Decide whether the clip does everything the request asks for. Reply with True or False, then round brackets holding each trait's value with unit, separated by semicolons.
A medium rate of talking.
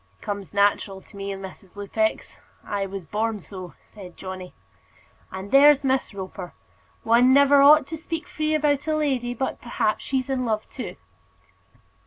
True (160 wpm)